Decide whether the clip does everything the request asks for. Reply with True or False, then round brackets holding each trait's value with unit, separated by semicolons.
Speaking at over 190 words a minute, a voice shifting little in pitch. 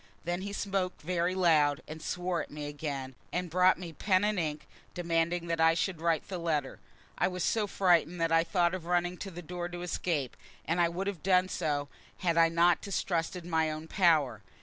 True (205 wpm; 2.1 semitones)